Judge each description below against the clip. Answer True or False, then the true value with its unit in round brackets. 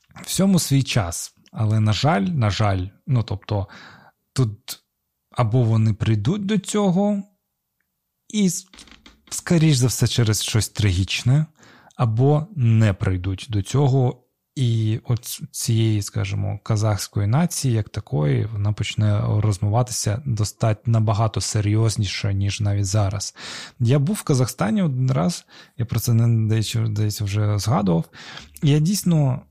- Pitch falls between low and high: False (115 Hz)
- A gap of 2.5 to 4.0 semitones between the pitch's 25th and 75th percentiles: False (4.7 semitones)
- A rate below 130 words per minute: True (120 wpm)